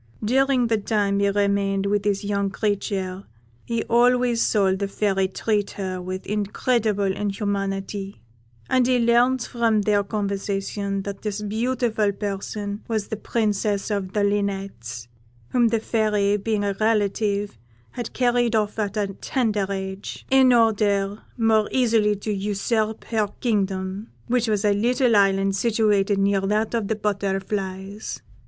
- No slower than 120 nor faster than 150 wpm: Yes, average, 145 wpm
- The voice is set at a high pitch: Yes, high, 205 Hz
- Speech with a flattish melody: Yes, narrow, 2.1 semitones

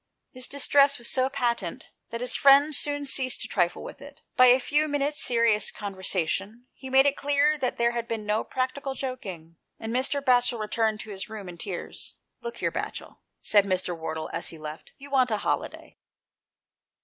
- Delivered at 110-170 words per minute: No, average, 195 wpm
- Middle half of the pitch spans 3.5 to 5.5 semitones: Yes, average, 5.1 semitones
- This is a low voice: No, high, 245 Hz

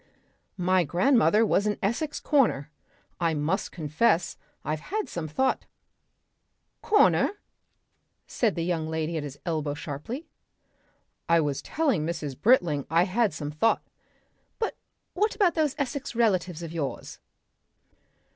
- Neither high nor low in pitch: Yes, medium, 175 Hz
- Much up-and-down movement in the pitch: Yes, wide, 7.2 semitones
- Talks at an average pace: No, slow, 130 wpm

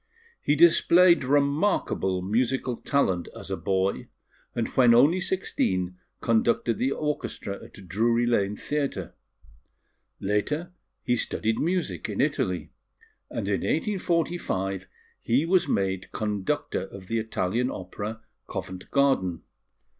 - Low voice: Yes, low, 115 Hz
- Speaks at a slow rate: Yes, slow, 115 wpm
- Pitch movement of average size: No, wide, 7.3 semitones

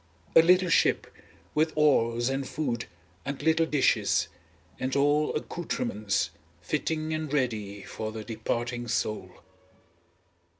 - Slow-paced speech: Yes, slow, 115 wpm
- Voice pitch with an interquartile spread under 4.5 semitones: No, average, 5.1 semitones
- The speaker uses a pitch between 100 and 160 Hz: Yes, low, 135 Hz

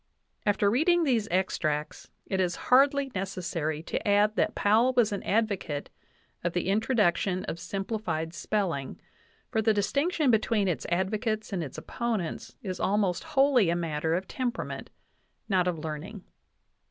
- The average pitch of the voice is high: Yes, high, 200 Hz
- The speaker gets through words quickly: No, average, 145 wpm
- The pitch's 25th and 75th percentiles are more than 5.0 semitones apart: No, average, 4.5 semitones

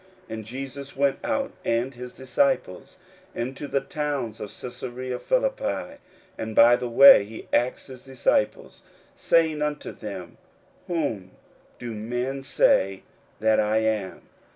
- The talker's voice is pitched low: Yes, low, 125 Hz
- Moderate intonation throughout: Yes, average, 4.1 semitones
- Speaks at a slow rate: Yes, slow, 130 wpm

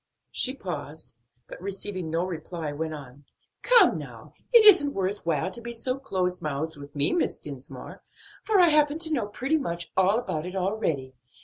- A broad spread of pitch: Yes, wide, 8.8 semitones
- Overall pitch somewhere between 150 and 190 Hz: Yes, medium, 185 Hz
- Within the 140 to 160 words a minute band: No, average, 180 wpm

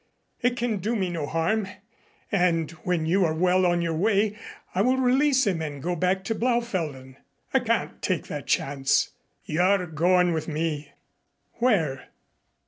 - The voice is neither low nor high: Yes, medium, 180 Hz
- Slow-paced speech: No, average, 155 wpm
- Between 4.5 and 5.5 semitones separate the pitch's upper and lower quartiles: Yes, average, 4.9 semitones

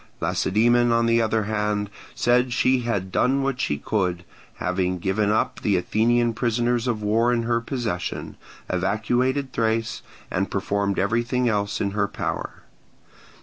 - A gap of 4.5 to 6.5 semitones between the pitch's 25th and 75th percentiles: No, average, 3.0 semitones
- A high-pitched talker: No, low, 110 Hz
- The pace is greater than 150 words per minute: No, average, 145 wpm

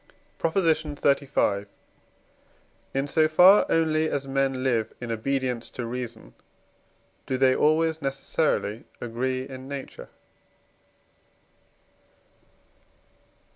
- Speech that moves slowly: Yes, slow, 90 wpm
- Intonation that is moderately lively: Yes, average, 3.8 semitones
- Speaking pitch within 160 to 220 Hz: No, low, 135 Hz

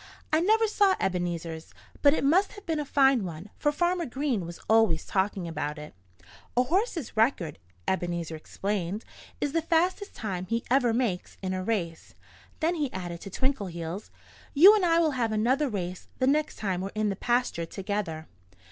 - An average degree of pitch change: No, wide, 8.8 semitones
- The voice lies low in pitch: No, high, 220 Hz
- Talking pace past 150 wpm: Yes, average, 175 wpm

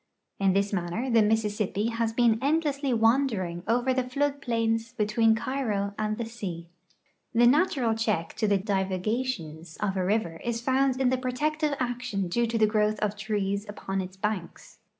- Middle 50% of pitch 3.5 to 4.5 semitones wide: Yes, average, 3.8 semitones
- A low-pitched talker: No, high, 225 Hz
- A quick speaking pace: No, average, 170 wpm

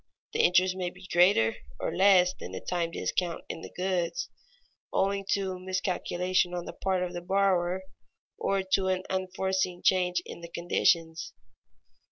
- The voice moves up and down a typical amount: No, narrow, 1.3 semitones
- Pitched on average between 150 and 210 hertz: Yes, medium, 185 Hz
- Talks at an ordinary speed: Yes, average, 155 wpm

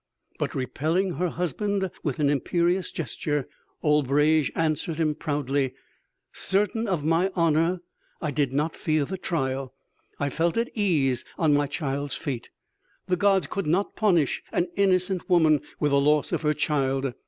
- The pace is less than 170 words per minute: Yes, average, 155 wpm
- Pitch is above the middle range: No, medium, 155 Hz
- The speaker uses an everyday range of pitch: Yes, average, 4.0 semitones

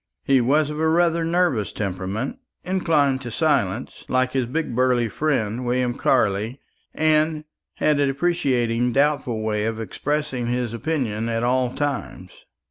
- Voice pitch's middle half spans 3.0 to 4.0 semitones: No, average, 4.6 semitones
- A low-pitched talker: Yes, low, 130 Hz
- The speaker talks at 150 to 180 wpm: No, average, 140 wpm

